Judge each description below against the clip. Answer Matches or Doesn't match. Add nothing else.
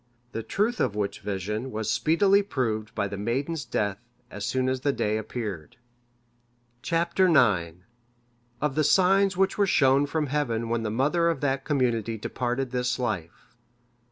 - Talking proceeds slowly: Doesn't match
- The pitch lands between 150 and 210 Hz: Doesn't match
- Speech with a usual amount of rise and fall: Doesn't match